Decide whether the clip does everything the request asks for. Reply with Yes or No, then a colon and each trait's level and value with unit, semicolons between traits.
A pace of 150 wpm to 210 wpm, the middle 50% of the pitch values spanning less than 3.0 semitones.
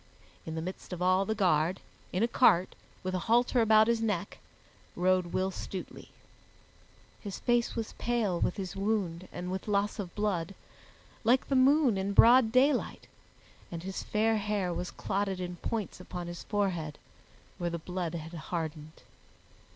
No: average, 160 wpm; average, 3.8 semitones